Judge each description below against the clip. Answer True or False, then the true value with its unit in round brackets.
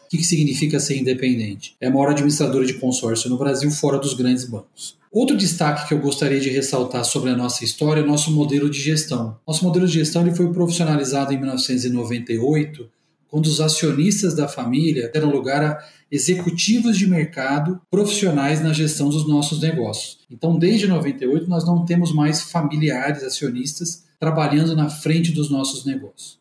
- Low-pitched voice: False (150 Hz)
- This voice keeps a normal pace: True (170 wpm)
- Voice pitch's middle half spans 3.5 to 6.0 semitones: False (3.0 semitones)